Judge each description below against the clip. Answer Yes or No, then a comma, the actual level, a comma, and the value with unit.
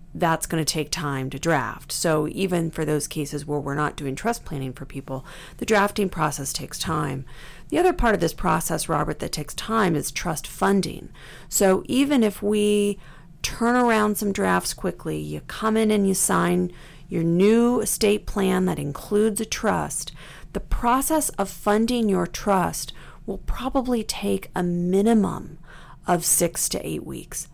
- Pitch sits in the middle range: Yes, medium, 175 Hz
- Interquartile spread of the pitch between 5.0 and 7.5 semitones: Yes, wide, 5.6 semitones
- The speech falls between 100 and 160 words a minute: No, average, 170 wpm